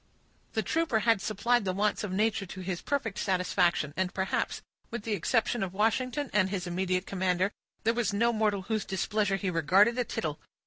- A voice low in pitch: No, high, 200 Hz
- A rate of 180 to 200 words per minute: Yes, average, 185 wpm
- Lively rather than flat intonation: No, average, 3.3 semitones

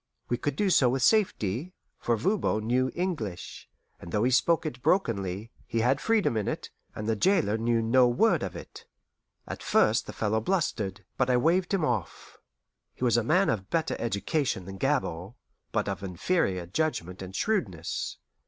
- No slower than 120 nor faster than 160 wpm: No, average, 175 wpm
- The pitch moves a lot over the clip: Yes, wide, 7.3 semitones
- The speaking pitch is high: No, low, 120 Hz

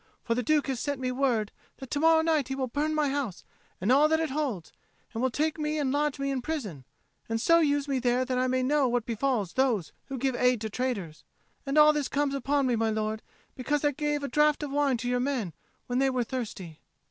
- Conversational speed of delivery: No, fast, 240 wpm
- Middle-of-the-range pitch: No, very high, 265 Hz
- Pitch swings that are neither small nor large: Yes, average, 3.3 semitones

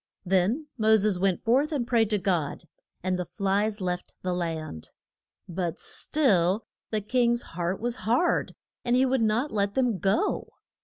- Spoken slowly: No, average, 160 wpm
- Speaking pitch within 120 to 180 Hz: No, high, 210 Hz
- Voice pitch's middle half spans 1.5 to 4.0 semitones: No, average, 4.8 semitones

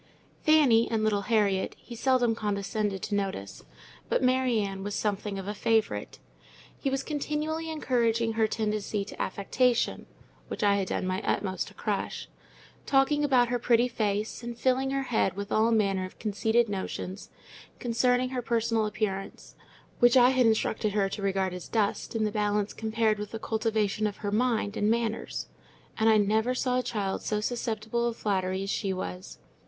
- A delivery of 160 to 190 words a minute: Yes, average, 175 wpm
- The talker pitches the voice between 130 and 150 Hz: No, high, 220 Hz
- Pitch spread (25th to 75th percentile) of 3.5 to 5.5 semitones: No, average, 3.0 semitones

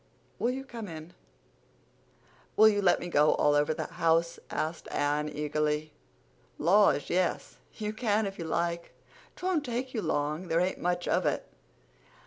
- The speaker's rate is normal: Yes, average, 150 wpm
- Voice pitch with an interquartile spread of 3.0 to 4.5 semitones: No, wide, 5.6 semitones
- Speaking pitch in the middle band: Yes, medium, 170 Hz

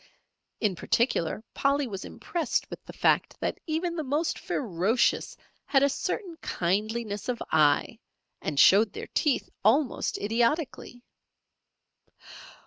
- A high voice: Yes, high, 235 Hz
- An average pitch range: No, wide, 6.2 semitones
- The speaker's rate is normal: No, slow, 120 wpm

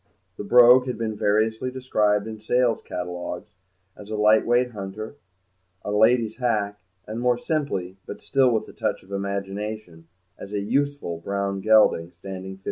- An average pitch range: Yes, average, 3.5 semitones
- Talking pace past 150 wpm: Yes, average, 160 wpm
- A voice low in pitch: Yes, low, 105 Hz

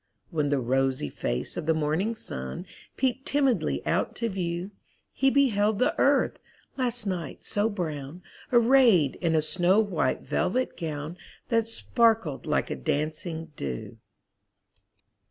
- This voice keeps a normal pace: No, slow, 130 wpm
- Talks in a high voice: No, medium, 180 Hz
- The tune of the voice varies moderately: No, wide, 7.2 semitones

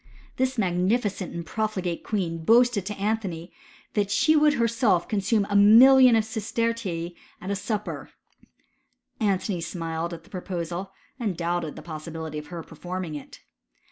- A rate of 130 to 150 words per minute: Yes, average, 145 wpm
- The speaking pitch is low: No, high, 195 Hz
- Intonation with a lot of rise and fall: No, average, 4.5 semitones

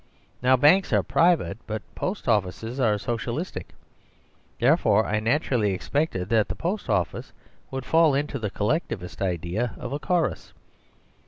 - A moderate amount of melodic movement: No, wide, 6.2 semitones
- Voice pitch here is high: No, low, 120 Hz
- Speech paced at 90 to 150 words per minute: Yes, average, 140 wpm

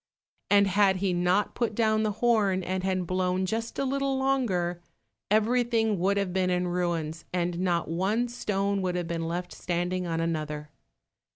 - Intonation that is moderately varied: Yes, average, 3.5 semitones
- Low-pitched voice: No, medium, 185 Hz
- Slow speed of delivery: No, average, 170 wpm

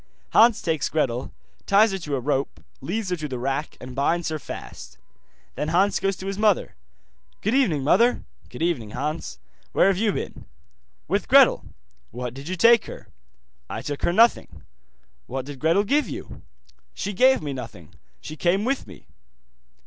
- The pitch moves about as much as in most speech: No, wide, 6.9 semitones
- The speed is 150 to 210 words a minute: Yes, average, 170 wpm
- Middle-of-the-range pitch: Yes, medium, 165 Hz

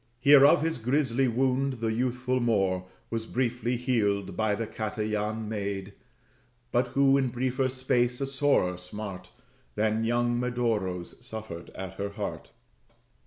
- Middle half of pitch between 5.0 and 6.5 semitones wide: No, average, 3.7 semitones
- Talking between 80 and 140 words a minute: Yes, slow, 135 wpm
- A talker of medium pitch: No, low, 115 Hz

